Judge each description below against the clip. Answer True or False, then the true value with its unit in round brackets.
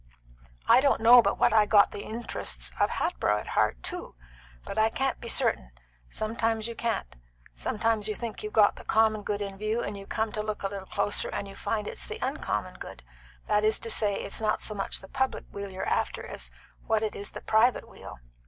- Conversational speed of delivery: False (220 wpm)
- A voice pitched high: True (215 Hz)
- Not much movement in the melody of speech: True (1.9 semitones)